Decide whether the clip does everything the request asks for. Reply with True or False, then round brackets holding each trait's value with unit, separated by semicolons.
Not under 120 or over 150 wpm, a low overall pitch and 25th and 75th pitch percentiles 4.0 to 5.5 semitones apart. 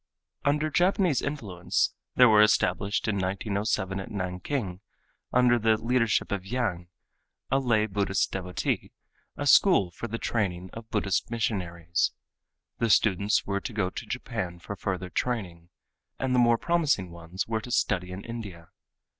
True (145 wpm; 105 Hz; 4.3 semitones)